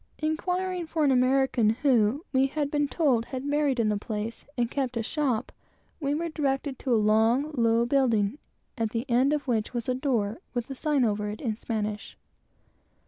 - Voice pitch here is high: Yes, very high, 255 Hz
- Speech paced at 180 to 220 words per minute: Yes, average, 190 wpm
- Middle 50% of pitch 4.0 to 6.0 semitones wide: Yes, average, 4.3 semitones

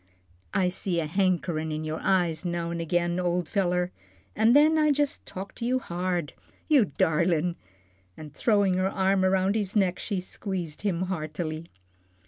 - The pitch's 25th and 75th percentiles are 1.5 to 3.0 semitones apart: Yes, average, 2.7 semitones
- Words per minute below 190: Yes, average, 160 wpm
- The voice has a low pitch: No, medium, 180 Hz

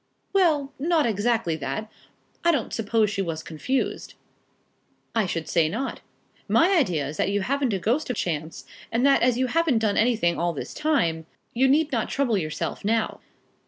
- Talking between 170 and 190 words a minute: Yes, average, 175 wpm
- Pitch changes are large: Yes, wide, 7.9 semitones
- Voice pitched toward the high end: Yes, high, 225 Hz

